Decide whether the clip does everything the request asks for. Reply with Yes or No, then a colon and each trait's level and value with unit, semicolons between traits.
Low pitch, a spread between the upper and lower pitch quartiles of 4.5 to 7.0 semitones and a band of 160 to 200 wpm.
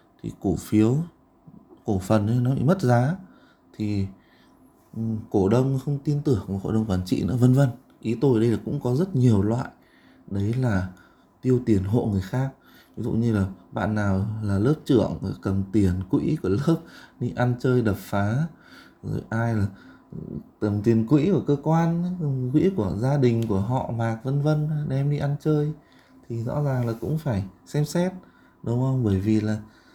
Yes: low, 120 Hz; average, 5.2 semitones; average, 190 wpm